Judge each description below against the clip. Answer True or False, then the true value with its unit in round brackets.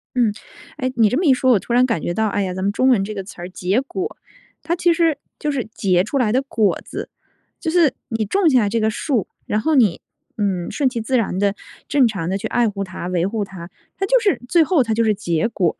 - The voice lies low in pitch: False (225 Hz)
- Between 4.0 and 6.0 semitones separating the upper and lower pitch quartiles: True (5.5 semitones)